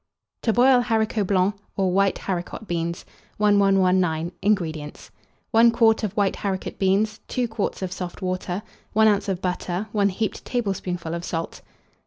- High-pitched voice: Yes, high, 195 Hz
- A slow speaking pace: No, average, 150 wpm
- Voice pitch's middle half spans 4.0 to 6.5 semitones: No, average, 3.2 semitones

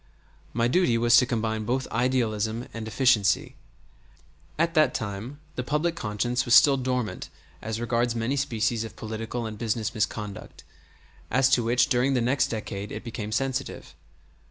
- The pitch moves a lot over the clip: No, narrow, 2.6 semitones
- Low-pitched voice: Yes, low, 120 Hz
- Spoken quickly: No, average, 155 wpm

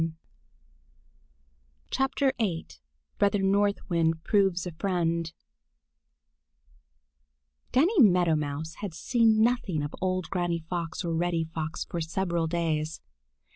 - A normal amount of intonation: Yes, average, 3.6 semitones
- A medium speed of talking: No, slow, 100 wpm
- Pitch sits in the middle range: Yes, medium, 170 Hz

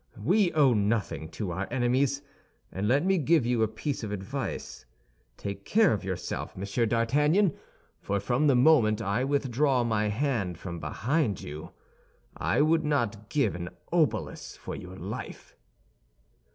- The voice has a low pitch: Yes, low, 120 Hz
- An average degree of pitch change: No, wide, 6.2 semitones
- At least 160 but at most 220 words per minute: No, average, 150 wpm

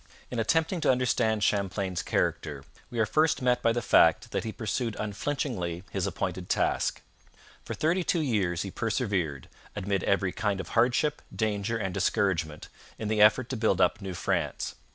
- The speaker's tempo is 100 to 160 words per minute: No, average, 170 wpm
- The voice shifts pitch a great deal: No, average, 4.3 semitones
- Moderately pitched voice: No, low, 110 Hz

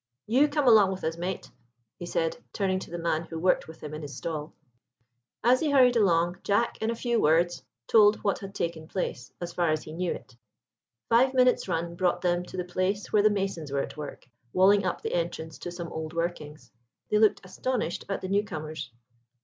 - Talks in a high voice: No, medium, 180 Hz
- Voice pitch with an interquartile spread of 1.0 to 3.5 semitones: No, average, 4.1 semitones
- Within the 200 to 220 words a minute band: Yes, fast, 205 wpm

